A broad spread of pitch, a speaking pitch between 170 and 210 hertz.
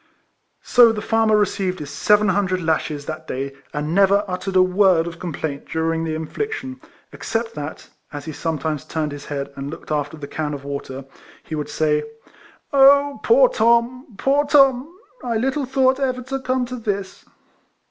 Yes: wide, 8.4 semitones; high, 190 Hz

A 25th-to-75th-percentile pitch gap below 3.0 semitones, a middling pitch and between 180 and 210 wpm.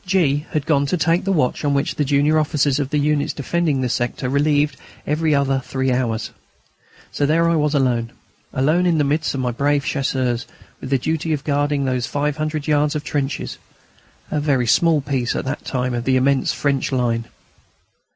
Yes: narrow, 2.5 semitones; medium, 145 Hz; average, 200 wpm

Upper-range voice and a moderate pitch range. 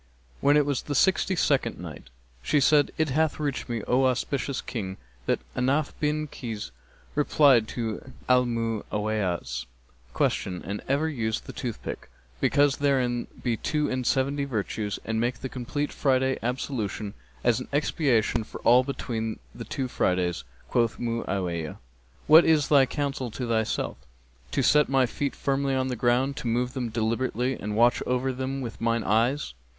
No: low, 125 Hz; average, 3.8 semitones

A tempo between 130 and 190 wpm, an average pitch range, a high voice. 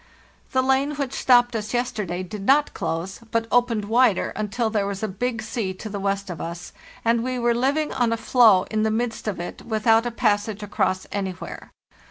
No: fast, 205 wpm; average, 3.4 semitones; high, 220 Hz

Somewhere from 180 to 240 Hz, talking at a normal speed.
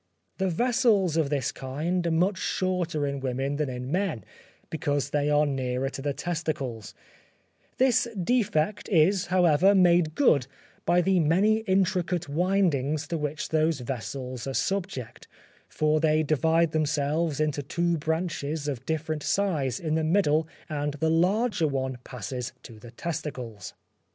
No: medium, 155 Hz; average, 145 wpm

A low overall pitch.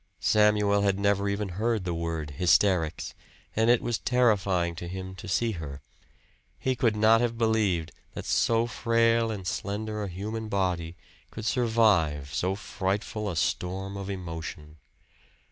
Yes: low, 100 Hz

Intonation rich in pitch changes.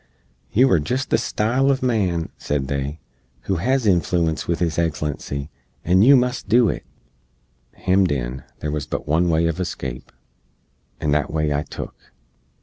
Yes: wide, 6.2 semitones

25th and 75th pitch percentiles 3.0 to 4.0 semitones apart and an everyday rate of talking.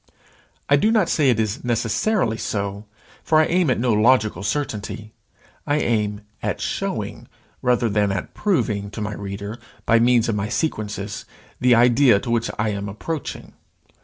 Yes: average, 3.6 semitones; average, 160 wpm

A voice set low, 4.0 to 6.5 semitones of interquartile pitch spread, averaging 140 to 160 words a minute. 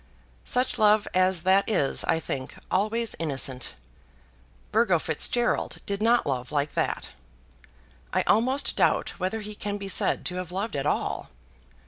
No: high, 195 Hz; average, 5.1 semitones; average, 145 wpm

